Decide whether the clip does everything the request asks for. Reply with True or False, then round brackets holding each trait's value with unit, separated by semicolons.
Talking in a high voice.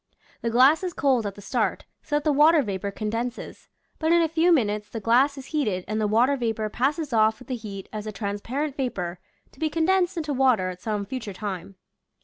True (240 Hz)